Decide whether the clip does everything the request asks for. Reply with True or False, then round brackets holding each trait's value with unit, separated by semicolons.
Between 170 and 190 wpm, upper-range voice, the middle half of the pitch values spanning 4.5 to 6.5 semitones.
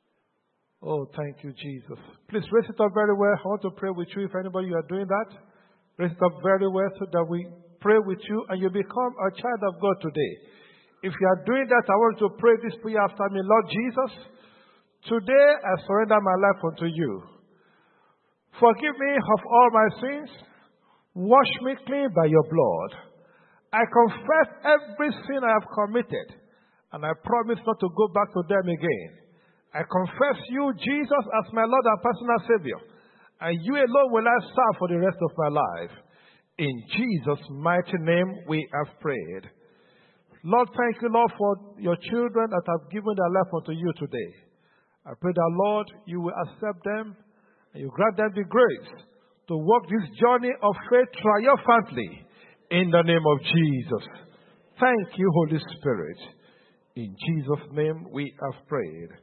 True (175 wpm; 200 Hz; 5.2 semitones)